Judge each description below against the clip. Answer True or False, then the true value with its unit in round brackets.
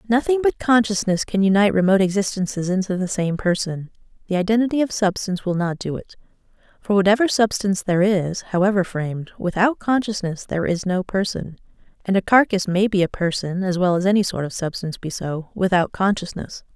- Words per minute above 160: True (180 wpm)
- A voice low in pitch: False (195 Hz)